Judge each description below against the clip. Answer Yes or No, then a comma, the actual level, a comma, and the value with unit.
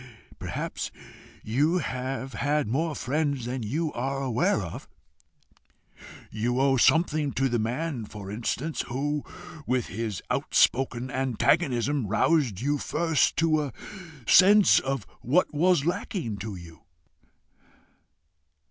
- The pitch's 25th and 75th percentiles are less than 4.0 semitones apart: No, average, 4.5 semitones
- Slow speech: Yes, slow, 115 wpm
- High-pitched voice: No, low, 135 Hz